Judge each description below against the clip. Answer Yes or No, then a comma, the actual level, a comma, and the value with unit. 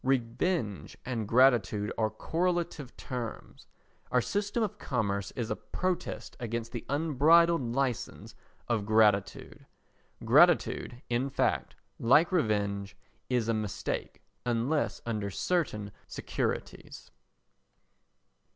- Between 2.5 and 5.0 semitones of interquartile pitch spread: No, wide, 5.4 semitones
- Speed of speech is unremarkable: No, slow, 100 wpm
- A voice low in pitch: Yes, low, 120 Hz